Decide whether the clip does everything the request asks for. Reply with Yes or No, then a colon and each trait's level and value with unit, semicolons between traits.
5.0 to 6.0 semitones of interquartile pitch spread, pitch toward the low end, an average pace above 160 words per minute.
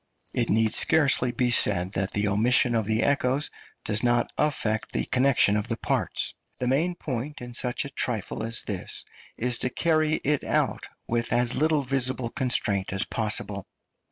No: average, 3.8 semitones; low, 120 Hz; average, 170 wpm